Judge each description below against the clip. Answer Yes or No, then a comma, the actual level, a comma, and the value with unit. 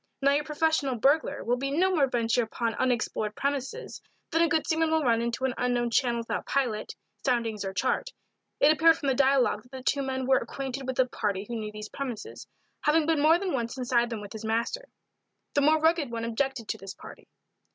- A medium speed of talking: No, fast, 210 wpm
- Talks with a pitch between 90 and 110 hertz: No, very high, 260 Hz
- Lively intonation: No, average, 3.9 semitones